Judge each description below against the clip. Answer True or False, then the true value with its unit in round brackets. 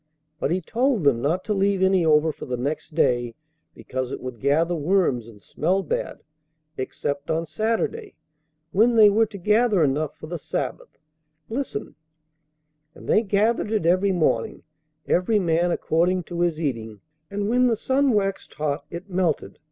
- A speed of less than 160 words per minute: False (165 wpm)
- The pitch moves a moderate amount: False (5.8 semitones)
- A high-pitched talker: False (175 Hz)